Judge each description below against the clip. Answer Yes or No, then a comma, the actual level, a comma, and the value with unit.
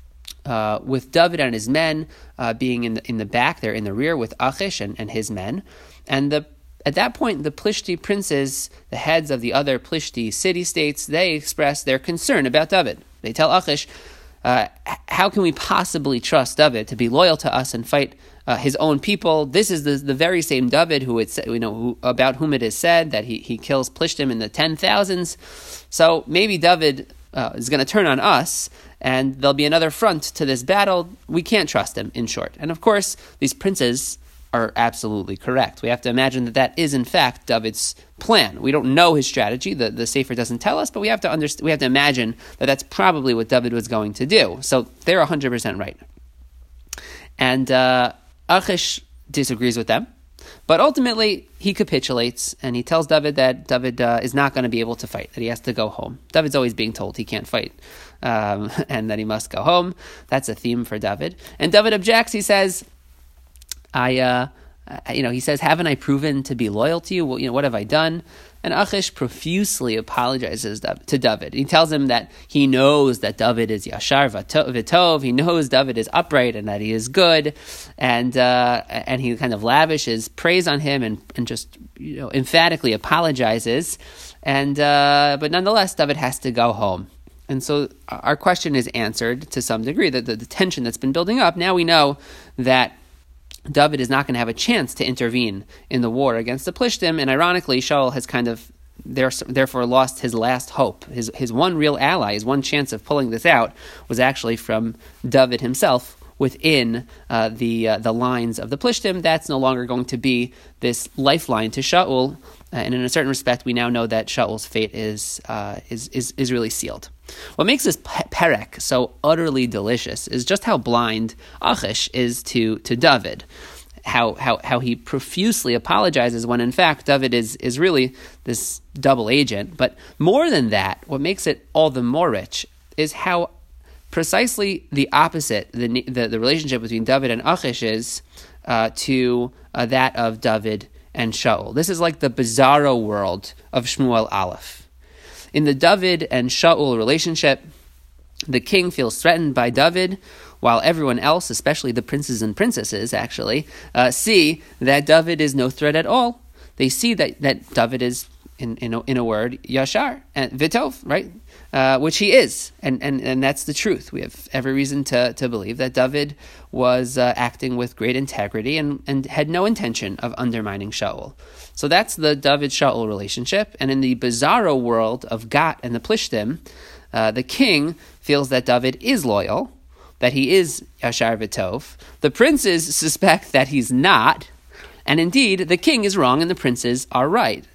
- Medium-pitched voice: No, low, 130 Hz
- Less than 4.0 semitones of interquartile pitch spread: No, average, 4.7 semitones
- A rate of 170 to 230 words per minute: Yes, average, 190 wpm